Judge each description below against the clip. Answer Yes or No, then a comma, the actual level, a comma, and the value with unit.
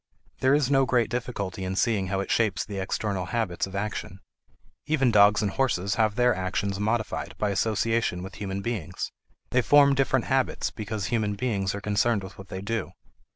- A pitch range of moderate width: Yes, average, 3.5 semitones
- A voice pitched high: No, low, 105 Hz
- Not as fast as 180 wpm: No, average, 185 wpm